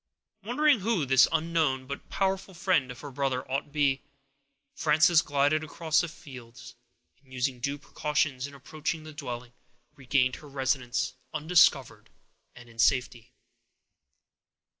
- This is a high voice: No, medium, 140 Hz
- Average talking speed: No, slow, 130 wpm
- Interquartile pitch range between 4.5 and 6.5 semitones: No, average, 3.4 semitones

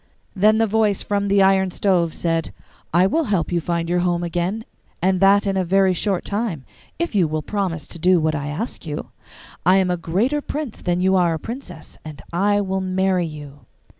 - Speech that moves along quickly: Yes, fast, 210 wpm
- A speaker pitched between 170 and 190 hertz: Yes, medium, 185 Hz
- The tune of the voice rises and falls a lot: No, average, 3.0 semitones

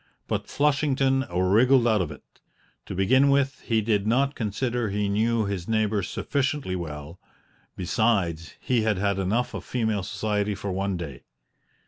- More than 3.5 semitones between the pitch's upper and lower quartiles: Yes, average, 4.6 semitones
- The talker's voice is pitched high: No, low, 105 Hz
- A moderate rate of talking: Yes, average, 150 wpm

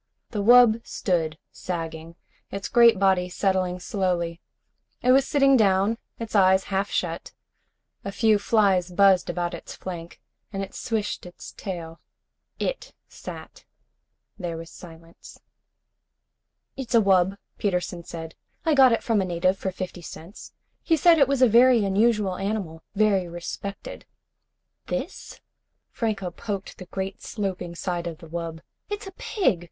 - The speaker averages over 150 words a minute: No, average, 145 wpm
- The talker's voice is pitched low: No, high, 190 Hz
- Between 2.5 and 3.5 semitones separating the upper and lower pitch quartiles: No, average, 4.0 semitones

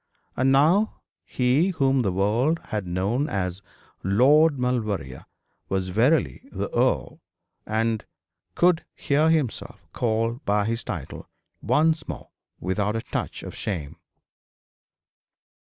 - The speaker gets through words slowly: Yes, slow, 115 wpm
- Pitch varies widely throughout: Yes, wide, 6.5 semitones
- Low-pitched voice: Yes, low, 115 Hz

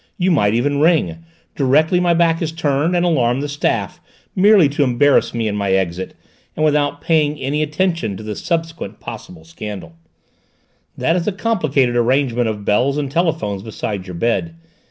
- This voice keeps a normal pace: Yes, average, 170 wpm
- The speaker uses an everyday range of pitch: No, wide, 6.8 semitones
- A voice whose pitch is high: No, medium, 145 Hz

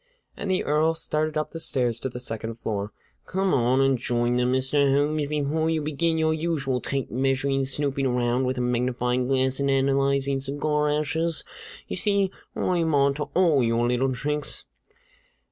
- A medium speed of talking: Yes, average, 175 wpm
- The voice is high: No, medium, 140 Hz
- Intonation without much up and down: No, average, 3.3 semitones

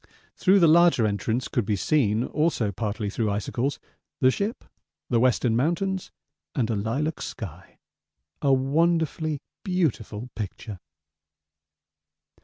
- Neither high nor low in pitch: No, low, 125 Hz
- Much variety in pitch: Yes, wide, 6.7 semitones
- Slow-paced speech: Yes, slow, 115 wpm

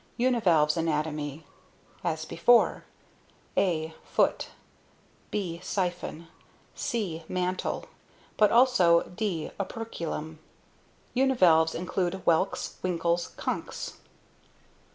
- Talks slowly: Yes, slow, 75 wpm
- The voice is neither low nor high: Yes, medium, 175 Hz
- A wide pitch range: No, average, 3.7 semitones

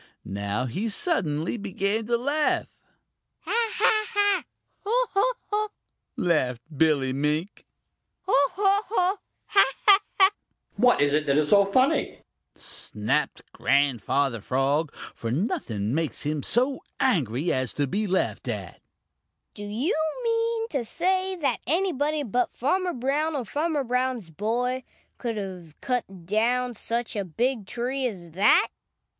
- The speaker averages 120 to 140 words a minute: Yes, slow, 135 wpm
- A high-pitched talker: Yes, high, 230 Hz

